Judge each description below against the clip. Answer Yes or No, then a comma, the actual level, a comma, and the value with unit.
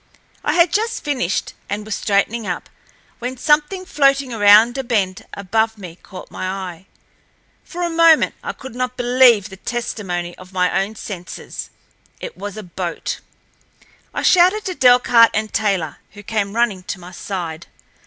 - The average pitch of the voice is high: Yes, high, 220 Hz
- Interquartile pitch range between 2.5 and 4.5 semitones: No, average, 5.2 semitones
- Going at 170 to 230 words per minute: No, average, 160 wpm